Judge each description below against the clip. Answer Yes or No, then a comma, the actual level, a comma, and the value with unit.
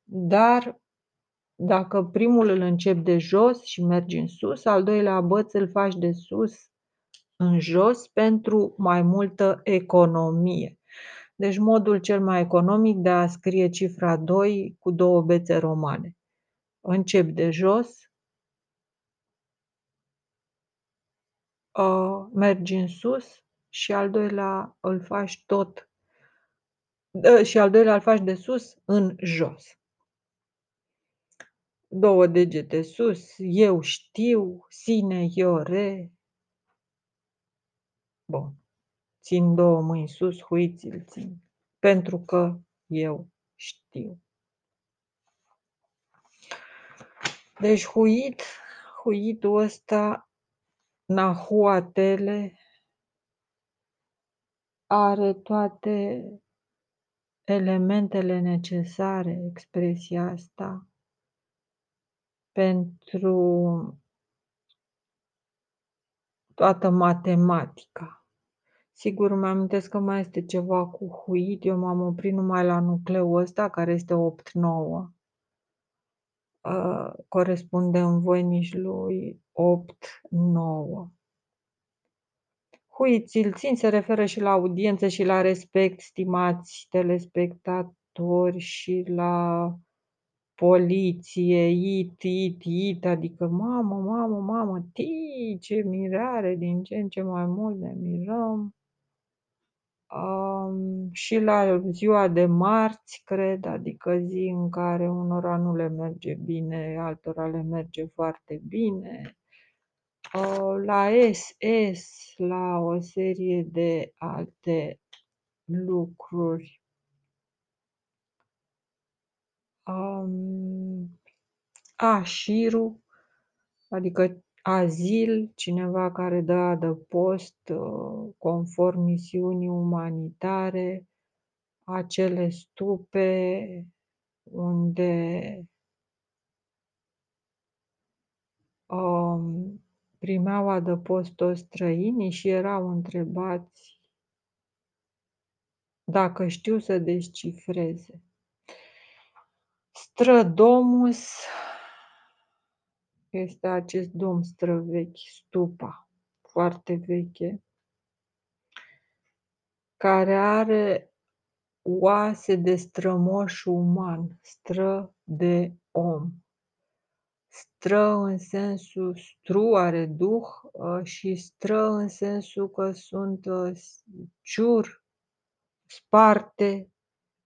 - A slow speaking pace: Yes, slow, 80 wpm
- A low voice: No, medium, 185 Hz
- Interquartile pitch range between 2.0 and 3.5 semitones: Yes, narrow, 2.4 semitones